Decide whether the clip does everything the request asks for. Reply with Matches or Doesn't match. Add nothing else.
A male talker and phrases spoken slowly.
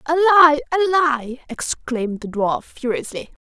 Doesn't match